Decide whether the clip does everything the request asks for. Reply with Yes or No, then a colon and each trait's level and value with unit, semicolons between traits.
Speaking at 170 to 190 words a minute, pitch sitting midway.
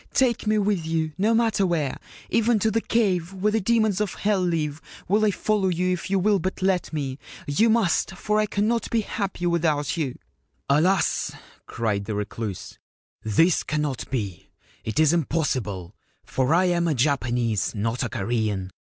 Yes: average, 180 wpm; medium, 170 Hz